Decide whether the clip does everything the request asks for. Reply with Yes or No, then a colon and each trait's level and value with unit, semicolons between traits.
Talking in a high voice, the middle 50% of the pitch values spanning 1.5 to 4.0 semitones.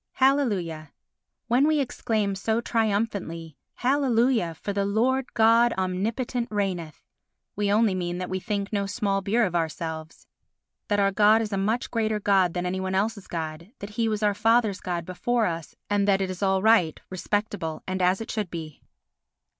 Yes: high, 200 Hz; average, 3.6 semitones